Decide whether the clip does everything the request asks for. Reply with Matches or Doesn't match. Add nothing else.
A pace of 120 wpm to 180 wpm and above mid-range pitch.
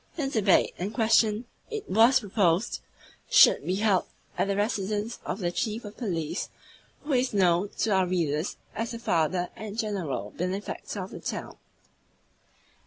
Matches